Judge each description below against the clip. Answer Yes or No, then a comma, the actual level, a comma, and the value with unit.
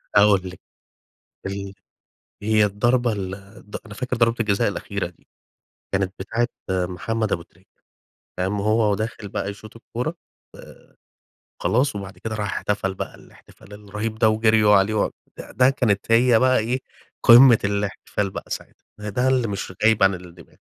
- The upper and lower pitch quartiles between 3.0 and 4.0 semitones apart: No, narrow, 2.6 semitones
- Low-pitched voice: Yes, low, 105 Hz